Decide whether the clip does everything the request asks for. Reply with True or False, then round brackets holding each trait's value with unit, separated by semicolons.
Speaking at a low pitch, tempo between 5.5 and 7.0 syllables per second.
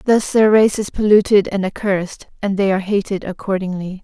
False (200 Hz; 5.6 syllables/s)